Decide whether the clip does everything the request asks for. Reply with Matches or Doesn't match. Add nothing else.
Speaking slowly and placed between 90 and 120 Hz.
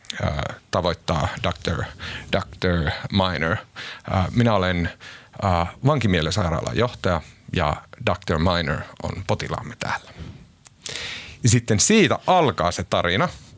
Matches